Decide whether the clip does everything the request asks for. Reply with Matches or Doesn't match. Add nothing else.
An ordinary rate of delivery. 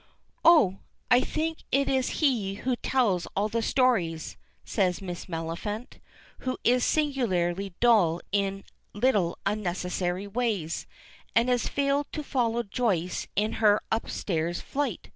Doesn't match